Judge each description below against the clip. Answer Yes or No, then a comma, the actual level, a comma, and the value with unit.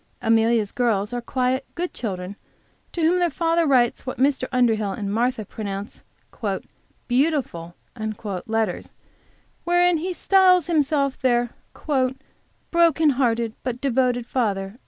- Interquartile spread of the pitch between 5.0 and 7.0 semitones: Yes, wide, 5.6 semitones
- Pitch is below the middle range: No, very high, 250 Hz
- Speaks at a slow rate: Yes, slow, 125 wpm